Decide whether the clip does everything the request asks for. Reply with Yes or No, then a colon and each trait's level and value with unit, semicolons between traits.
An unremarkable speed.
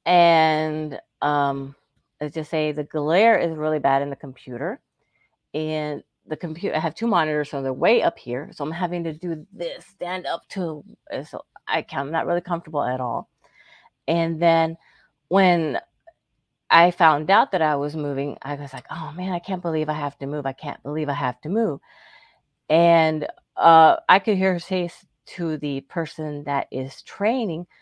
Yes: average, 185 wpm